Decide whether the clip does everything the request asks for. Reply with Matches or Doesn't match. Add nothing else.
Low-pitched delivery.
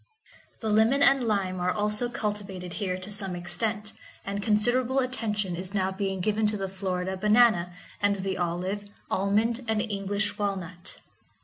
Doesn't match